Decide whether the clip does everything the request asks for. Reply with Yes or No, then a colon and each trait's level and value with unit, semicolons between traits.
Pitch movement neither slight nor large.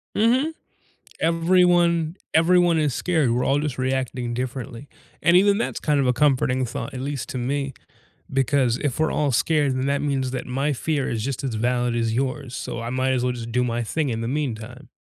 Yes: average, 3.5 semitones